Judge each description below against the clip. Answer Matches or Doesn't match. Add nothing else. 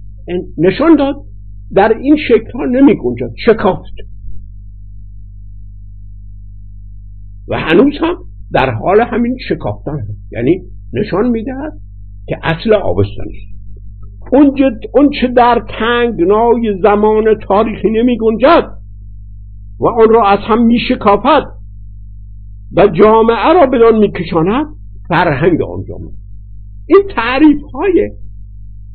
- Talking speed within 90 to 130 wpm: Matches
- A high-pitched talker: Doesn't match